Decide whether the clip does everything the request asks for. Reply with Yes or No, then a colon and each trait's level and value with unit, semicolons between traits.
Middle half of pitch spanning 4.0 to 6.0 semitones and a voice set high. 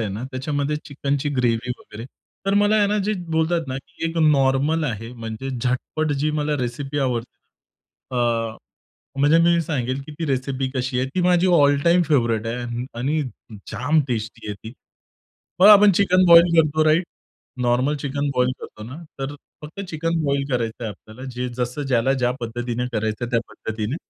No: average, 4.5 semitones; low, 135 Hz